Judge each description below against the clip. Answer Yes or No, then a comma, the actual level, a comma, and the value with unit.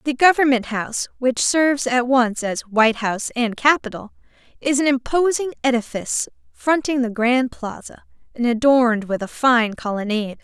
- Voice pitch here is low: No, very high, 250 Hz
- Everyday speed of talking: Yes, average, 150 wpm